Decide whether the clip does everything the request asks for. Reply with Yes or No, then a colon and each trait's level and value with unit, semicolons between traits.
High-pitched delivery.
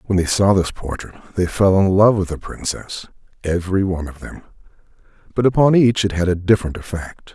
No: very low, 95 Hz